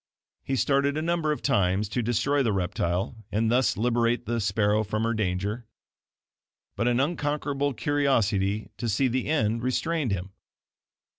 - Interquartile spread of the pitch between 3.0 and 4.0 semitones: No, average, 5.0 semitones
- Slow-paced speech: No, average, 150 wpm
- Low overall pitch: Yes, low, 115 Hz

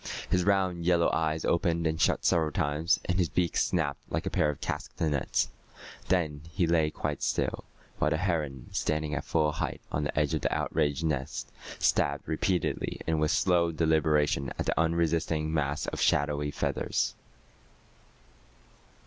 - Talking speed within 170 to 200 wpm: No, average, 155 wpm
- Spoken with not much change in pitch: Yes, narrow, 2.2 semitones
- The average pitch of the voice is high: No, very low, 80 Hz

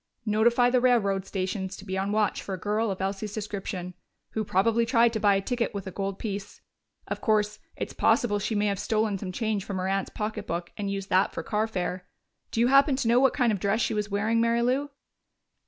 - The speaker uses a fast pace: Yes, fast, 220 wpm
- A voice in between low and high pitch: No, high, 210 Hz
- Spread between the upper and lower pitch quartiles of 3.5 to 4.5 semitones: No, average, 2.8 semitones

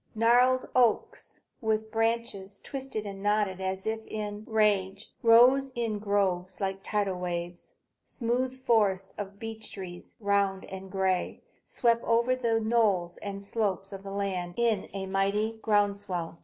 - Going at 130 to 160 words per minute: Yes, average, 140 wpm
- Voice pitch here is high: Yes, high, 205 Hz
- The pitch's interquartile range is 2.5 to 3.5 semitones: Yes, average, 2.9 semitones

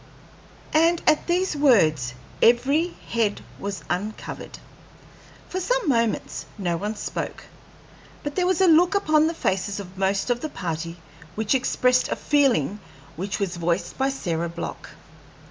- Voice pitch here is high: Yes, high, 230 Hz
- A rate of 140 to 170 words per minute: Yes, average, 145 wpm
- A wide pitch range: Yes, wide, 8.7 semitones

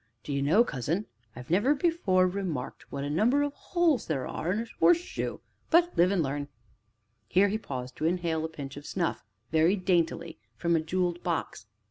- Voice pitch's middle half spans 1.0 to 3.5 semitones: No, wide, 5.4 semitones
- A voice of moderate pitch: Yes, medium, 175 Hz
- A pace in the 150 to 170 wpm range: No, average, 180 wpm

